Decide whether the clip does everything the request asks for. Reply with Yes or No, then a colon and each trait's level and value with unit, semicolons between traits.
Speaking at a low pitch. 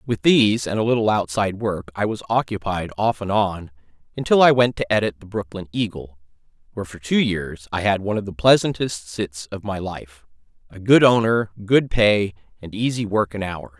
Yes: low, 100 Hz